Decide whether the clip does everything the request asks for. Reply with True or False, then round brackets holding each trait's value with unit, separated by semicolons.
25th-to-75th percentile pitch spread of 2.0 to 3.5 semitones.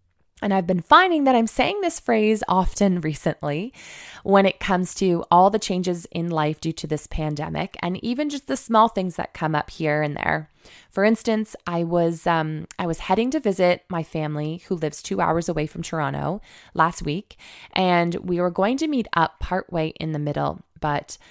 False (4.2 semitones)